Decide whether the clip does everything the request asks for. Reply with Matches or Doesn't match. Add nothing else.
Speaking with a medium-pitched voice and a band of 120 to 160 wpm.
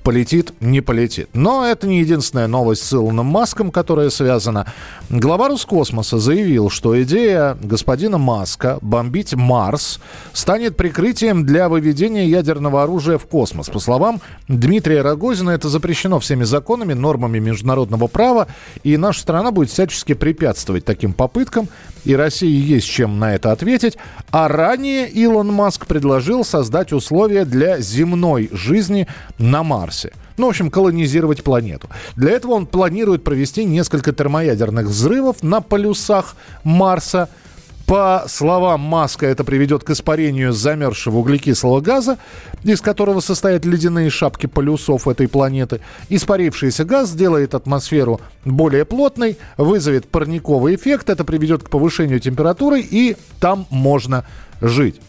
Matches